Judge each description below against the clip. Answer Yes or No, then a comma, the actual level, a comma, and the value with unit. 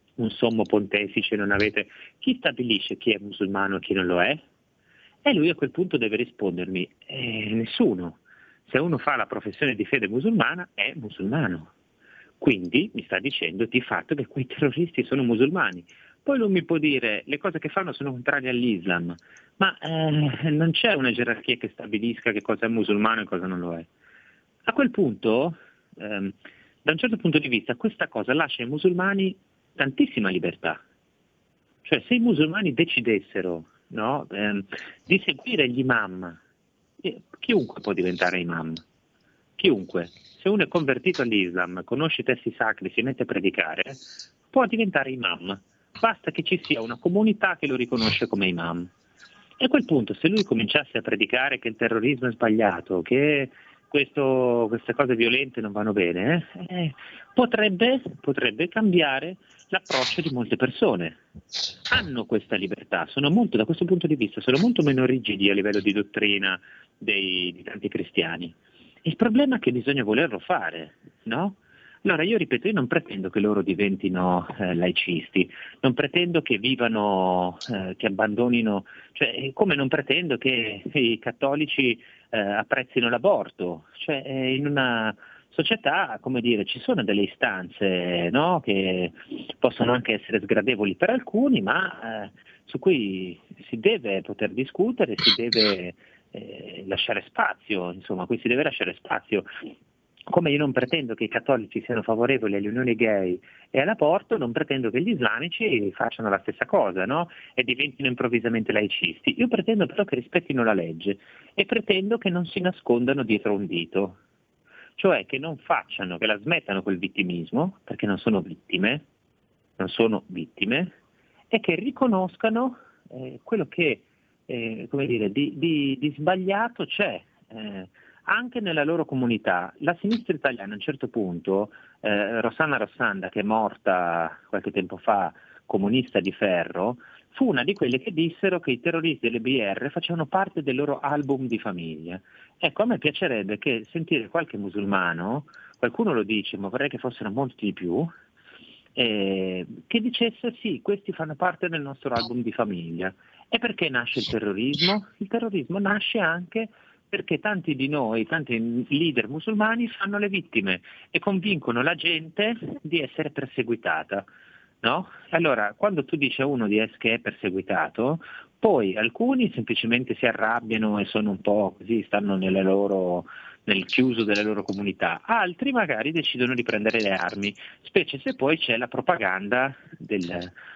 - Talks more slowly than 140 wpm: No, average, 155 wpm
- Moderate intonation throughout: No, wide, 8.2 semitones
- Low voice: Yes, low, 125 Hz